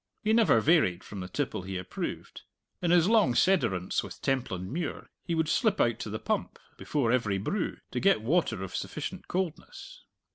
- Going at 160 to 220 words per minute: Yes, average, 175 wpm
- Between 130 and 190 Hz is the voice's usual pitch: Yes, low, 135 Hz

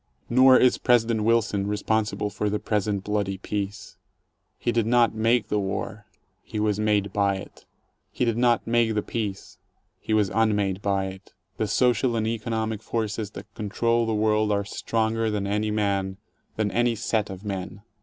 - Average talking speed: Yes, average, 170 wpm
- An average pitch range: No, narrow, 1.9 semitones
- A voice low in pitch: Yes, low, 105 Hz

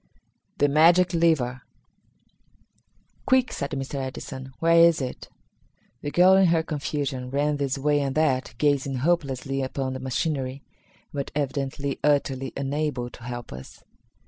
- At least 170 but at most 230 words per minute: No, slow, 135 wpm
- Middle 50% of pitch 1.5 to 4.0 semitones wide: Yes, average, 2.7 semitones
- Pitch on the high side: No, medium, 140 Hz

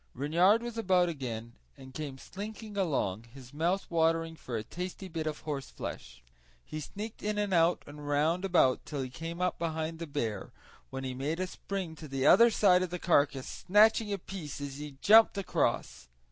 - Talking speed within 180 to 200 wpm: Yes, average, 190 wpm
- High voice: No, medium, 165 Hz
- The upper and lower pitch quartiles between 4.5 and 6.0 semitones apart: Yes, average, 5.2 semitones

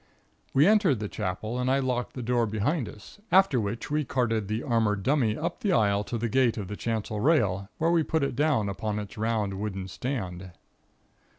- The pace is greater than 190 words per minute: Yes, average, 200 wpm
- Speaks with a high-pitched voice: No, low, 115 Hz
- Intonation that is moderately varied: Yes, average, 4.7 semitones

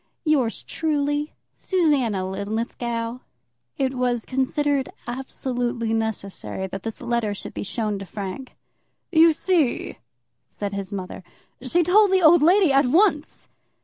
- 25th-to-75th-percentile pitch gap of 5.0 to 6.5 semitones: Yes, wide, 5.4 semitones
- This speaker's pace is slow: Yes, slow, 125 wpm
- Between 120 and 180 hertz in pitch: No, very high, 250 Hz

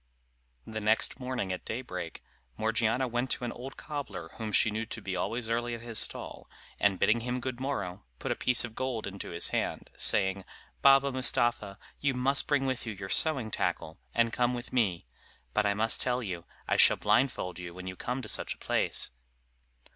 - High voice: No, low, 115 Hz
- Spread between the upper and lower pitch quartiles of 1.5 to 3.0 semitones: No, average, 4.0 semitones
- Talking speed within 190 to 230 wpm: Yes, average, 195 wpm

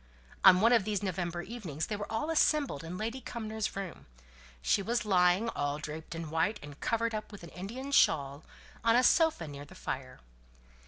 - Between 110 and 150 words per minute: No, average, 190 wpm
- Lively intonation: Yes, wide, 6.0 semitones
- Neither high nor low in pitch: No, high, 195 Hz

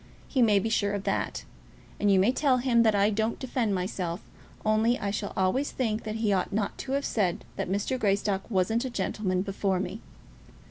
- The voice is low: No, high, 210 Hz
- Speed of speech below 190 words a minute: No, average, 200 wpm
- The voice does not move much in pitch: No, average, 3.0 semitones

